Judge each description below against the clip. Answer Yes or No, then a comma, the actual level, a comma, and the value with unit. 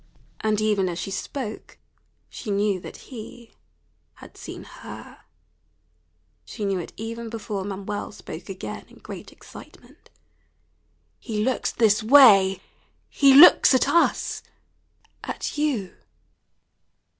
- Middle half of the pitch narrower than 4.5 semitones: Yes, average, 3.3 semitones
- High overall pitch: Yes, high, 215 Hz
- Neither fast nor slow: No, slow, 115 wpm